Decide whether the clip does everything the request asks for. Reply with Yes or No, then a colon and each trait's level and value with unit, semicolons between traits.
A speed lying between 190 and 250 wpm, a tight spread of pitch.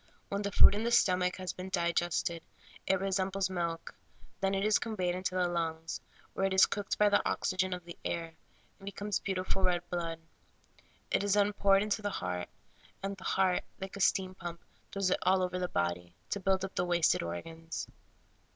Yes: average, 195 wpm; narrow, 2.3 semitones